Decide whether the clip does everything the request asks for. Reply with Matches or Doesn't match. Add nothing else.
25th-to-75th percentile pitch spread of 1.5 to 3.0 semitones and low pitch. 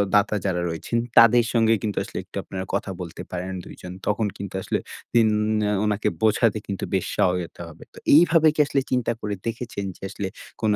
Doesn't match